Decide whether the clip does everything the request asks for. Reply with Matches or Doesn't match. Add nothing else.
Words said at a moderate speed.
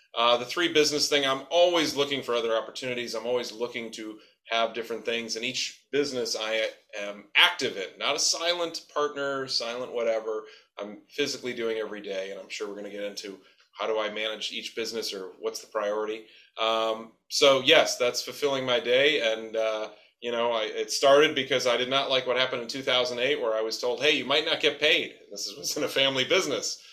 Doesn't match